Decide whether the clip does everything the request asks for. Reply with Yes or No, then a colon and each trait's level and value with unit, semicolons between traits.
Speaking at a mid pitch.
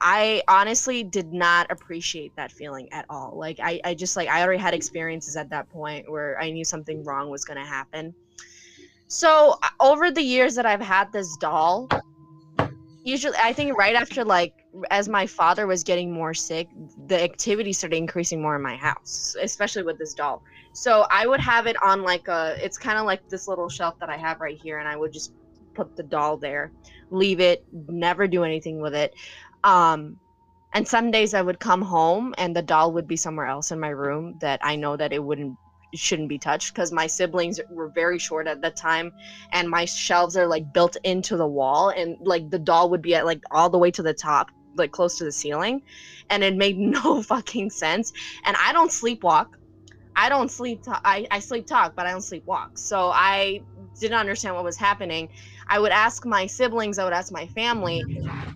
Yes: medium, 175 Hz